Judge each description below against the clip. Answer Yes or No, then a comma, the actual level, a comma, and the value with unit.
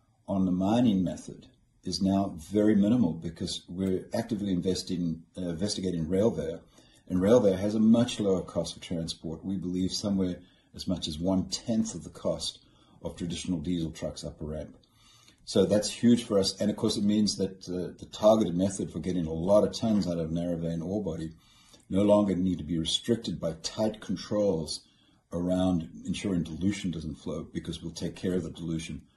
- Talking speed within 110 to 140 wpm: No, average, 185 wpm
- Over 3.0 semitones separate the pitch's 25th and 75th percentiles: Yes, average, 3.4 semitones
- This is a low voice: Yes, very low, 95 Hz